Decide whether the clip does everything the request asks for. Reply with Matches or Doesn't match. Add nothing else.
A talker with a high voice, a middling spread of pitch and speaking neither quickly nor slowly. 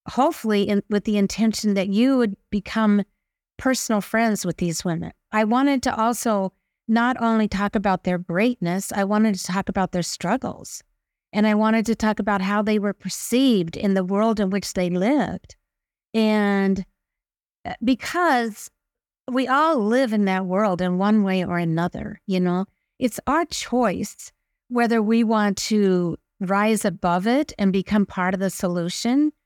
Matches